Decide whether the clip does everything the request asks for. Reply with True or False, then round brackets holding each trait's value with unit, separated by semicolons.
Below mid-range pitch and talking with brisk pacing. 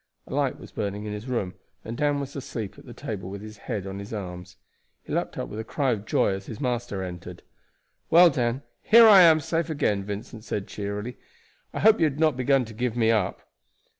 True (115 Hz; 225 wpm)